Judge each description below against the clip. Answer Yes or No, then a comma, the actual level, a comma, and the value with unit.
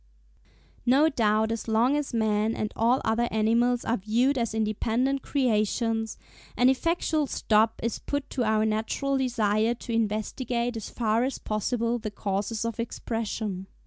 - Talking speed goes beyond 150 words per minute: No, average, 145 wpm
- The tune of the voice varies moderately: No, narrow, 2.3 semitones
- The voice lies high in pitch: Yes, high, 230 Hz